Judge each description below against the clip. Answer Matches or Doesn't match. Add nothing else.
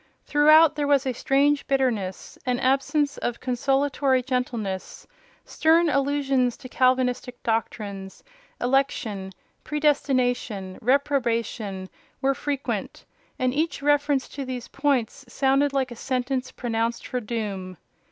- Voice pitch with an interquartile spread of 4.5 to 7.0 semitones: Doesn't match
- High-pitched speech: Matches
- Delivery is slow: Matches